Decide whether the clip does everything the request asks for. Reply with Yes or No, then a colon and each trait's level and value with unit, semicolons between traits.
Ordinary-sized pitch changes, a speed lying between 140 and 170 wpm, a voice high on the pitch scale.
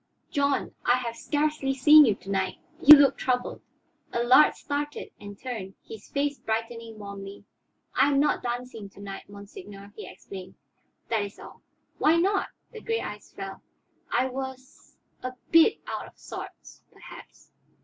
No: wide, 5.9 semitones; average, 150 wpm; very high, 250 Hz